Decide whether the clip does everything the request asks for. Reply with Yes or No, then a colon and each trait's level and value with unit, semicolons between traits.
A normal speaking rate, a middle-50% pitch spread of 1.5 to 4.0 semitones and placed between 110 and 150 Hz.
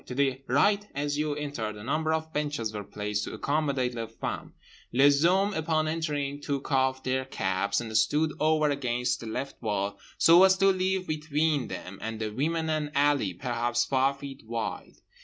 No: average, 180 wpm; average, 4.8 semitones; medium, 140 Hz